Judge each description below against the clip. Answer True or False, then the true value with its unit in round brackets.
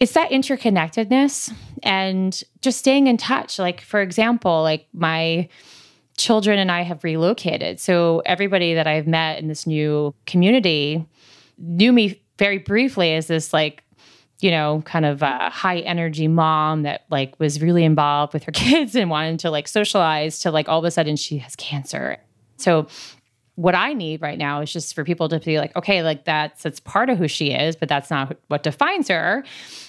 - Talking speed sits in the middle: True (185 wpm)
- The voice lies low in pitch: False (165 Hz)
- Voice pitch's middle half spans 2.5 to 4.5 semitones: True (3.5 semitones)